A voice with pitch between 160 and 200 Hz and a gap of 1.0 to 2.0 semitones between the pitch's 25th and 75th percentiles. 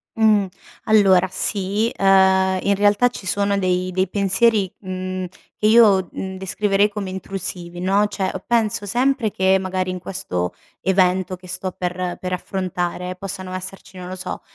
Yes: high, 190 Hz; narrow, 1.6 semitones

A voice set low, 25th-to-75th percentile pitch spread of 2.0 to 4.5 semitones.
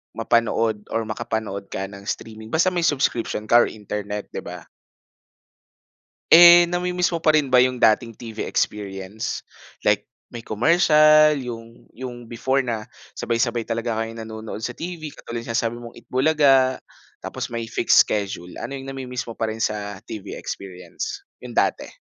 Yes: low, 115 Hz; average, 3.8 semitones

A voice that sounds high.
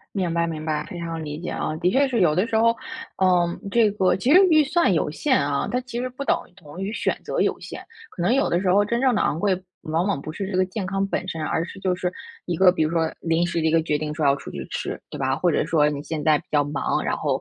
No: medium, 180 Hz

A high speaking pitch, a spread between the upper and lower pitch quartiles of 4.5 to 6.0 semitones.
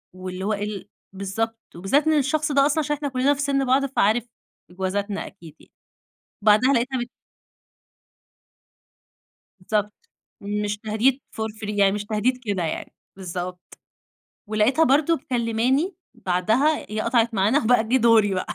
Yes: high, 225 Hz; average, 4.9 semitones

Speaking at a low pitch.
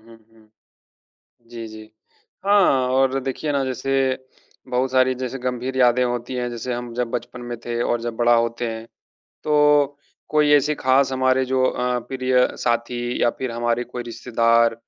Yes: low, 125 Hz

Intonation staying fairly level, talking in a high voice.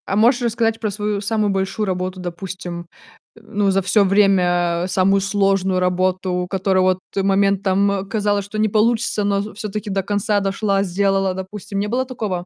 Yes: narrow, 2.0 semitones; high, 195 Hz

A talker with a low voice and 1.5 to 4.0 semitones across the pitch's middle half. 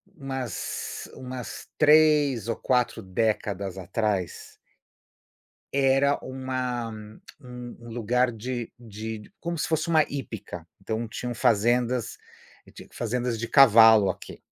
Yes: low, 120 Hz; average, 2.9 semitones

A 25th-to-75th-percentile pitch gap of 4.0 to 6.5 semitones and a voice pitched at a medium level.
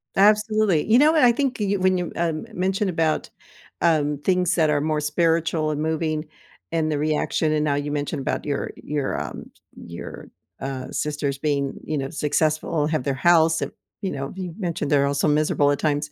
No: average, 3.2 semitones; medium, 155 Hz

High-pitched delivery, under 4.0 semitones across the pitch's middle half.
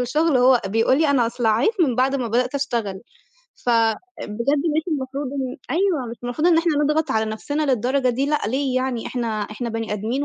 Yes: very high, 255 Hz; average, 3.6 semitones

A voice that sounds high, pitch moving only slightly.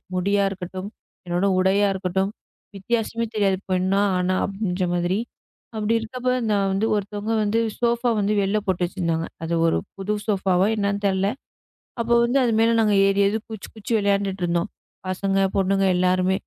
Yes: high, 195 Hz; narrow, 2.2 semitones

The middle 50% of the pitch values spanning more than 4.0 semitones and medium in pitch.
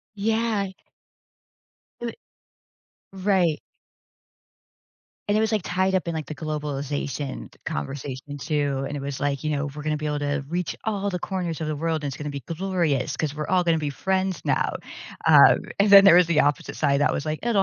Yes: average, 4.6 semitones; medium, 155 Hz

